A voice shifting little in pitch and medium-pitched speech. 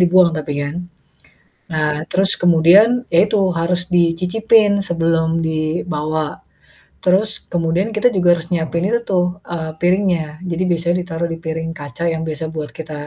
Yes: narrow, 2.1 semitones; medium, 170 Hz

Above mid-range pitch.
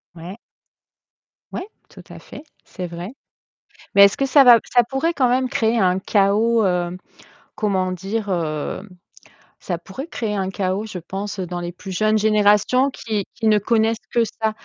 Yes: high, 205 Hz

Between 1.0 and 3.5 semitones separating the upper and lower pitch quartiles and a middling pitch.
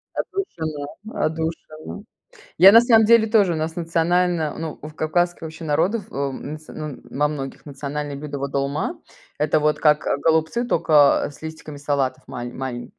Yes: average, 2.8 semitones; medium, 155 Hz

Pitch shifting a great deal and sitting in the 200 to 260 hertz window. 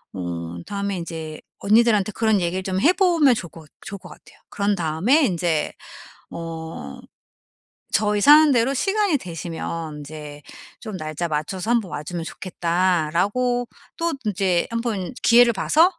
No: wide, 6.2 semitones; medium, 185 Hz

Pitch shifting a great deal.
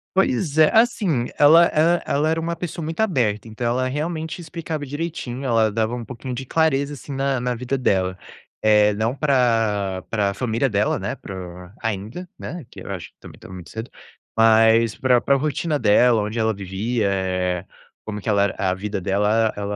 Yes: wide, 5.9 semitones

